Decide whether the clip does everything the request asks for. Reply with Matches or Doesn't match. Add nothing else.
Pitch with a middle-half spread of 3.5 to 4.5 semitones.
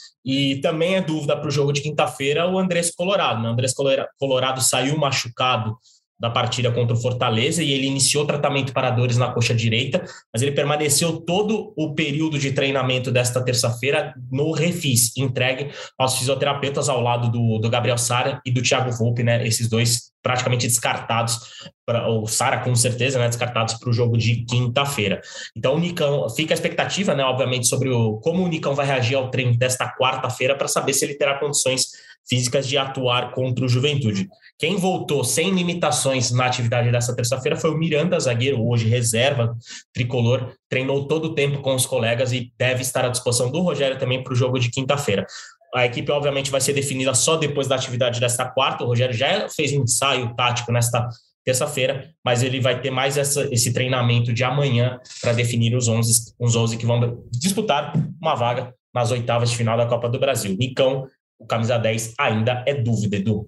Doesn't match